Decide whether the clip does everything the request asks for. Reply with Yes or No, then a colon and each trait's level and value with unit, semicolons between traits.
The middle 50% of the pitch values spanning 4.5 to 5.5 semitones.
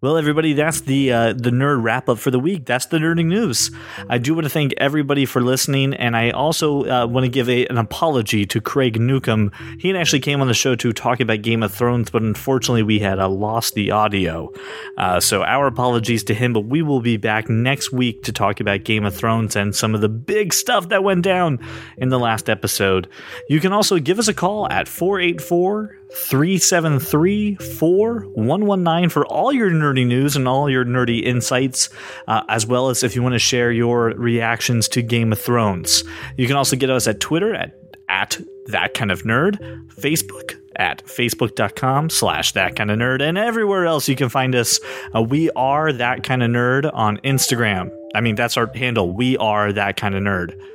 Yes: average, 4.8 semitones